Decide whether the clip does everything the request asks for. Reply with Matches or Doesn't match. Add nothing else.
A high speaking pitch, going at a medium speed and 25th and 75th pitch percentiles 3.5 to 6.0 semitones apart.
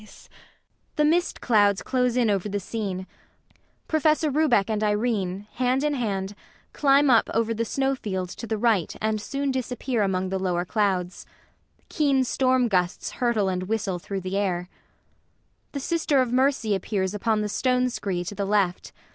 Matches